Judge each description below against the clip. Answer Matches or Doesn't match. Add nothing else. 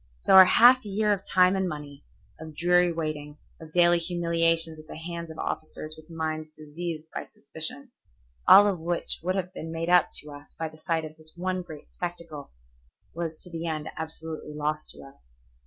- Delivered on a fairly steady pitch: Matches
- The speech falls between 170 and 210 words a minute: Matches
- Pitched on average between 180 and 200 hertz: Doesn't match